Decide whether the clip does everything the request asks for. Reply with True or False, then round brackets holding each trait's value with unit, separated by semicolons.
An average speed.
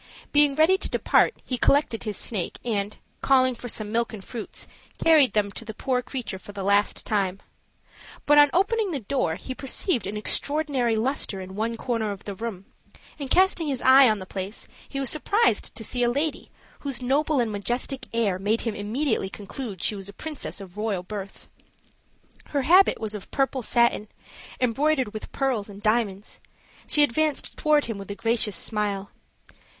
True (180 wpm)